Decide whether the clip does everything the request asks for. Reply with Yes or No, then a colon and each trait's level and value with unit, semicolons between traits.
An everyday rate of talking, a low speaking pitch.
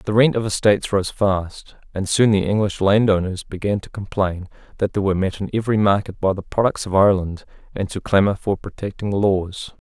Yes: average, 195 wpm; low, 100 Hz